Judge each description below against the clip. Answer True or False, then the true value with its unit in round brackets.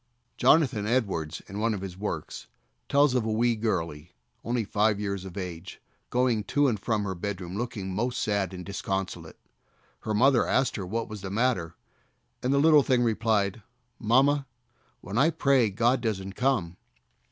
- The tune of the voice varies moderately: True (4.4 semitones)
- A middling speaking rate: True (165 wpm)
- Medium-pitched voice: False (110 Hz)